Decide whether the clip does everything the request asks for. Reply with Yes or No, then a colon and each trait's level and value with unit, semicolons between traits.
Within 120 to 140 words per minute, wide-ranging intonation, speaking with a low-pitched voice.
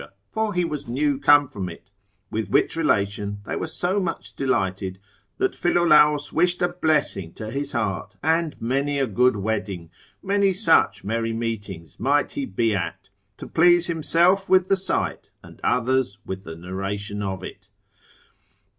No: average, 155 wpm; wide, 8.5 semitones; low, 130 Hz